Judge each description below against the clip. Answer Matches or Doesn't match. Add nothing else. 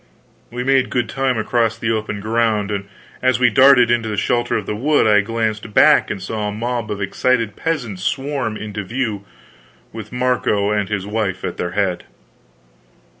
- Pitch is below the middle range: Matches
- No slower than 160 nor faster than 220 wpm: Matches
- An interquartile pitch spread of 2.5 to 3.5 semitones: Matches